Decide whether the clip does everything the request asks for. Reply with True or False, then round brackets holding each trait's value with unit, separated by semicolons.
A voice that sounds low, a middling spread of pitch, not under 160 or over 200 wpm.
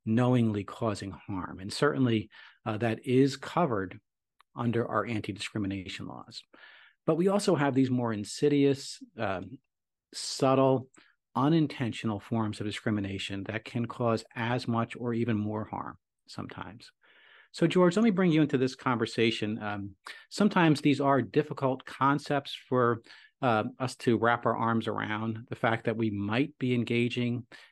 False (120 Hz; 3.8 semitones; 145 wpm)